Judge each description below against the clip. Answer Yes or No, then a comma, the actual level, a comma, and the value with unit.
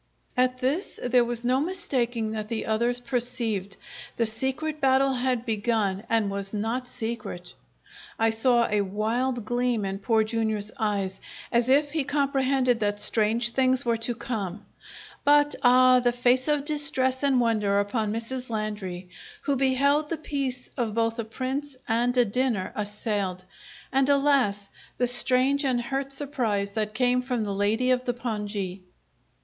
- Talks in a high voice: Yes, high, 240 Hz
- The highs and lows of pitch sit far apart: No, average, 3.3 semitones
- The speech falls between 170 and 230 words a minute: No, average, 155 wpm